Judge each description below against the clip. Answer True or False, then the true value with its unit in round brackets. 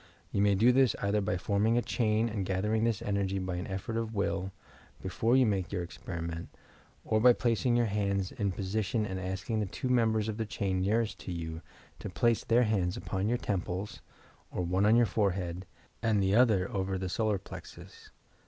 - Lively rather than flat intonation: False (3.0 semitones)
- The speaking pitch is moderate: False (100 Hz)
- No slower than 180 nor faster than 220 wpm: True (200 wpm)